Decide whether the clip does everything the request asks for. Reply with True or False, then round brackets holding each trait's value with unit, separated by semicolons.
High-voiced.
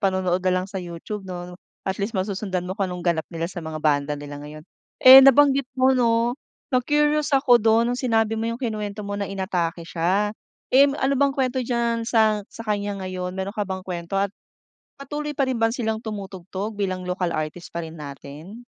True (200 Hz)